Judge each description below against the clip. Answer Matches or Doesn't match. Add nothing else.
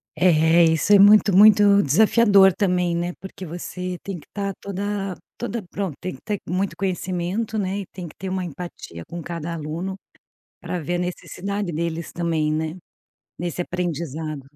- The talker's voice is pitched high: Doesn't match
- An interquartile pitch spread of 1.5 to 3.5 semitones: Matches